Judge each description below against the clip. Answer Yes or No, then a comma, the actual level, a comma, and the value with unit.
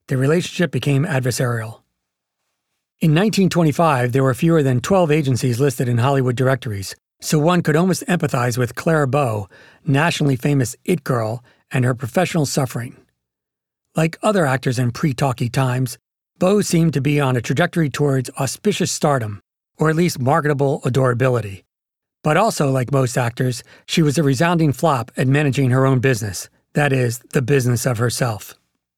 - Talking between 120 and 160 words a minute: Yes, average, 150 wpm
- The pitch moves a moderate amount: Yes, average, 3.9 semitones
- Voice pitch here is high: No, low, 135 Hz